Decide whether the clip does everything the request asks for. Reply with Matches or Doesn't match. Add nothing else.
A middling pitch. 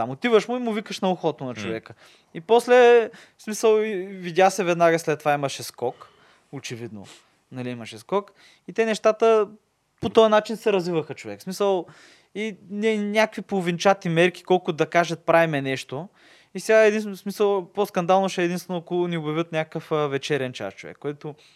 Matches